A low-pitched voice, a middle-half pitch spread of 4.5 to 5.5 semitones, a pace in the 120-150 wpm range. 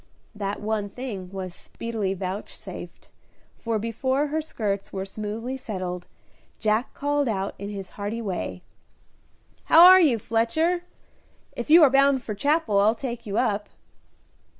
No: high, 220 Hz; average, 4.9 semitones; average, 140 wpm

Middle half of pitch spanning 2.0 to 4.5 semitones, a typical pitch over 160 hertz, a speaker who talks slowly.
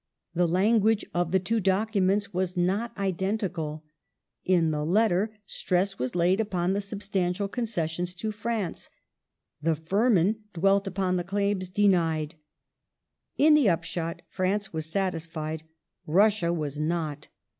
Yes: average, 3.4 semitones; medium, 185 Hz; slow, 125 wpm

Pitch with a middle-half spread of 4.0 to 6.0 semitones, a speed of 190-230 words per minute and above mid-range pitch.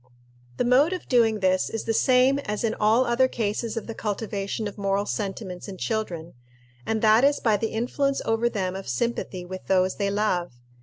No: average, 3.4 semitones; average, 195 wpm; high, 215 Hz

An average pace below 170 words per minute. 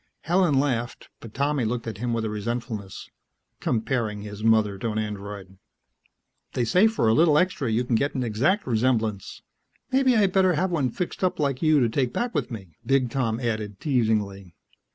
No: average, 185 wpm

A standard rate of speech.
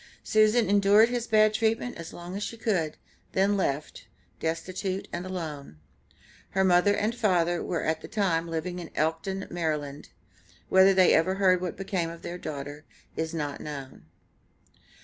Yes: average, 155 wpm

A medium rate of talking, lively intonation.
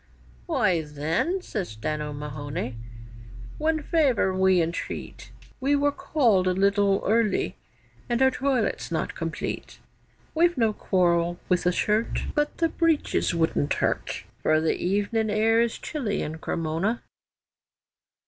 No: slow, 130 wpm; wide, 7.6 semitones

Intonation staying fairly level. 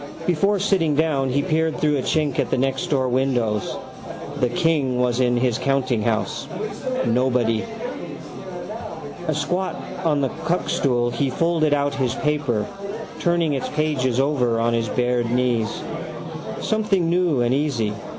No: average, 4.2 semitones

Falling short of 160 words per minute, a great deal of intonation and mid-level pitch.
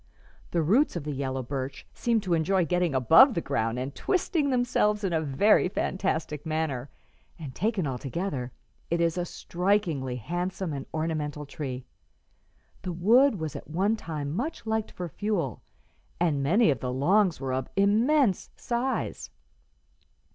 Yes: average, 150 wpm; wide, 6.6 semitones; medium, 170 Hz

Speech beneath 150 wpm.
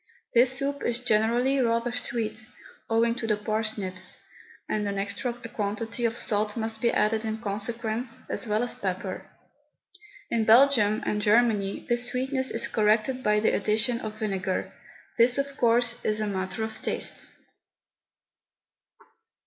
Yes: average, 140 wpm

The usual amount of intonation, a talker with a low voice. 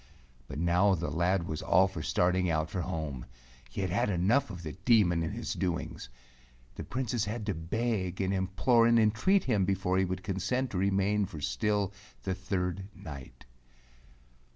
Yes: average, 3.2 semitones; very low, 95 Hz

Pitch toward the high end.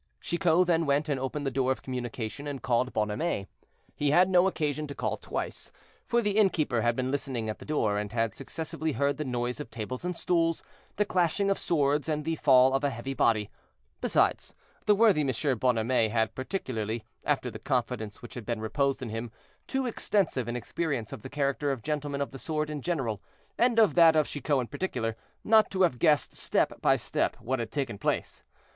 No: medium, 140 Hz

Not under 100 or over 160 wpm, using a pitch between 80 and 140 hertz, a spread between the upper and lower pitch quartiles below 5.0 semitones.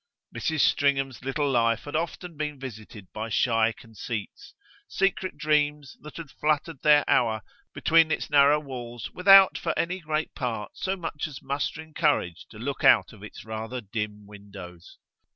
No: average, 155 wpm; low, 135 Hz; wide, 5.5 semitones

